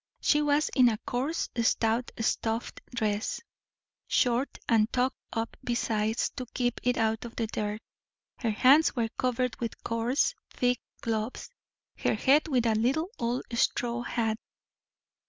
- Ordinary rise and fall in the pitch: No, narrow, 2.1 semitones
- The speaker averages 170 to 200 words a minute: No, average, 140 wpm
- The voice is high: Yes, high, 235 Hz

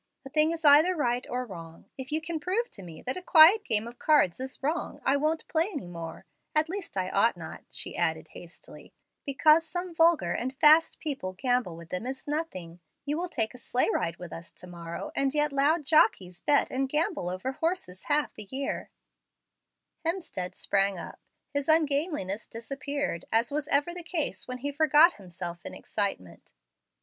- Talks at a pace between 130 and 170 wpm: No, average, 185 wpm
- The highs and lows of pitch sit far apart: Yes, wide, 8.1 semitones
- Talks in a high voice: Yes, very high, 275 Hz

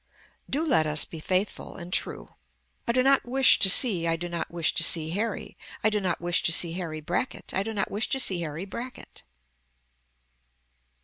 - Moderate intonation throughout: Yes, average, 5.0 semitones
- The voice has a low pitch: No, medium, 185 Hz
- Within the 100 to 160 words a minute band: No, average, 195 wpm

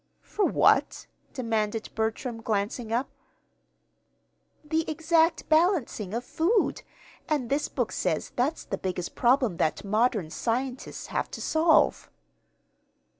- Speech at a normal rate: No, slow, 115 wpm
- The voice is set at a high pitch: Yes, high, 245 Hz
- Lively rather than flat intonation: Yes, wide, 6.3 semitones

